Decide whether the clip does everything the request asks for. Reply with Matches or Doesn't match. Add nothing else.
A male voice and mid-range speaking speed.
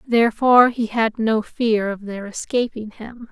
Doesn't match